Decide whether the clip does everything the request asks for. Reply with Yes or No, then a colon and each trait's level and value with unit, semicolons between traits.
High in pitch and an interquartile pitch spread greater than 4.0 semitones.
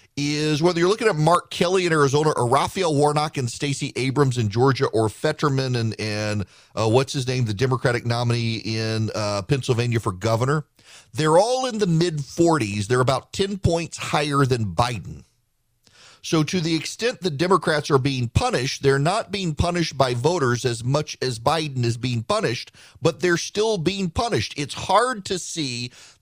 No: medium, 140 Hz; average, 5.3 semitones